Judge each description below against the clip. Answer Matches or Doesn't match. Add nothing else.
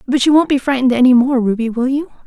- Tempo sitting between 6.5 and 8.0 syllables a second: Matches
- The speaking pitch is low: Doesn't match